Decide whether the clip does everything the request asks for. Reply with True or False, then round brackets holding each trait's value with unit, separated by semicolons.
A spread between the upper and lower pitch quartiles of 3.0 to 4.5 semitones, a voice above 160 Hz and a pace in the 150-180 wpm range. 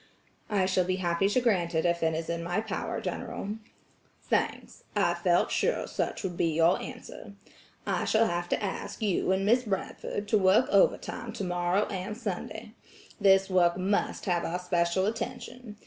True (3.3 semitones; 190 Hz; 170 wpm)